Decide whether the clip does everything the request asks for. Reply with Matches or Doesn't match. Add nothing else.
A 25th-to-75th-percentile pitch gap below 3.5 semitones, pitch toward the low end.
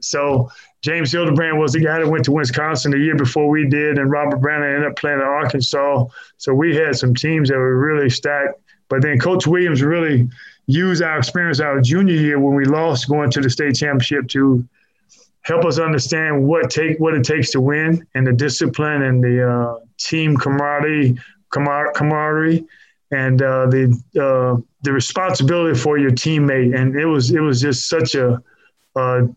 Doesn't match